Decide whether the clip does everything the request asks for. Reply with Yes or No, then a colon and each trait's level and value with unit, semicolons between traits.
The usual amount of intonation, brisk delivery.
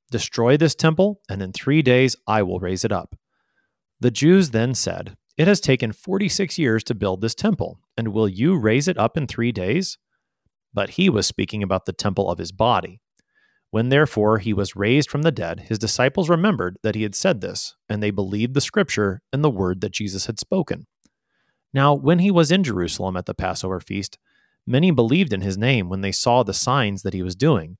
No: wide, 6.7 semitones; fast, 210 wpm